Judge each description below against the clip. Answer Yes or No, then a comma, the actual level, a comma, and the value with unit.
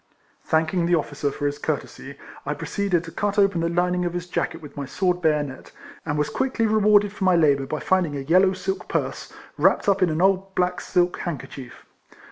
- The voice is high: No, medium, 175 Hz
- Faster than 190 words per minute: Yes, average, 200 wpm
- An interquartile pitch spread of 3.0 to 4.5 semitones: Yes, average, 4.0 semitones